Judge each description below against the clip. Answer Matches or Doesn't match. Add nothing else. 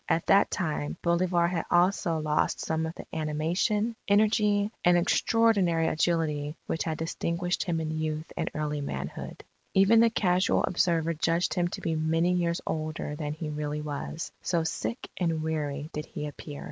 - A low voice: Doesn't match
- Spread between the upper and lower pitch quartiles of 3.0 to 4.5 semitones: Doesn't match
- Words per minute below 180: Matches